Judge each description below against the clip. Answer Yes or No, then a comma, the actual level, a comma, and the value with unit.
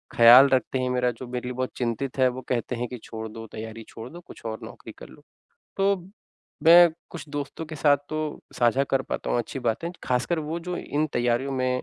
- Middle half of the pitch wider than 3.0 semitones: Yes, average, 3.7 semitones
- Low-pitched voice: Yes, low, 130 Hz